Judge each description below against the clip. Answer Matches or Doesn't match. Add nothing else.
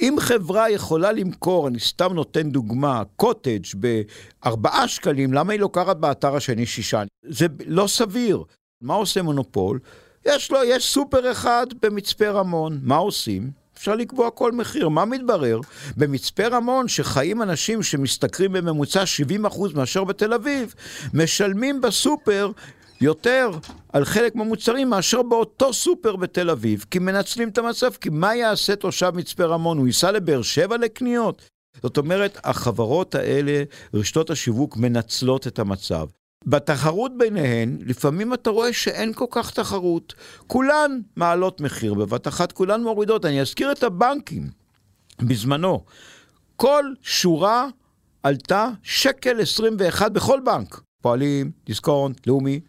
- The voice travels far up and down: Matches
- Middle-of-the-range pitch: Matches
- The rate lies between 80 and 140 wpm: Matches